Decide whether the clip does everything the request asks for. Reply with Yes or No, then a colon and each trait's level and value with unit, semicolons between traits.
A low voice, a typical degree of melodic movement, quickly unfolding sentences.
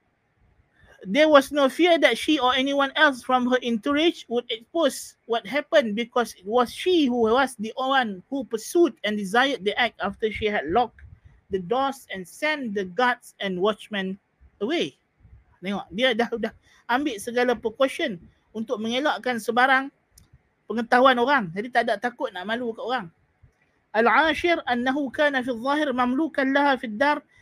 No: very high, 250 Hz; average, 3.7 semitones; fast, 160 wpm